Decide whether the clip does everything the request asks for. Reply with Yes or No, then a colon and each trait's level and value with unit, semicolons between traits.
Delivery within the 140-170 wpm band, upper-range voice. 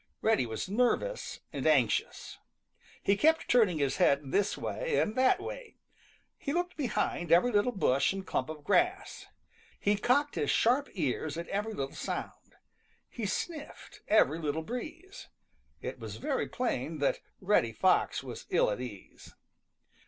Yes: average, 150 wpm; high, 210 Hz